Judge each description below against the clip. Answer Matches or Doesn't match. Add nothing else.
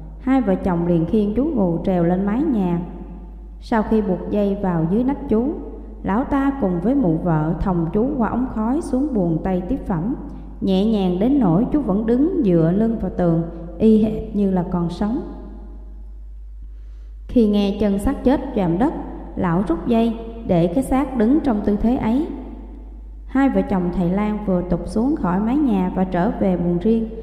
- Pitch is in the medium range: Doesn't match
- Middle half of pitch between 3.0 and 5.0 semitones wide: Doesn't match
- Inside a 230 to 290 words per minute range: Doesn't match